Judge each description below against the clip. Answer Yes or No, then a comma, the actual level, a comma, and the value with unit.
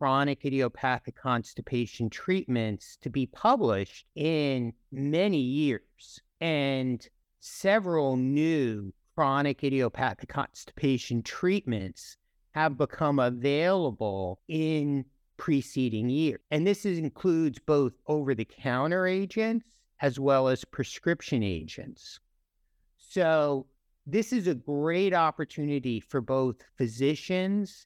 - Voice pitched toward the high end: No, medium, 140 Hz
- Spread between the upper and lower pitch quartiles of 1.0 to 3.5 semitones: No, average, 4.0 semitones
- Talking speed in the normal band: No, slow, 95 wpm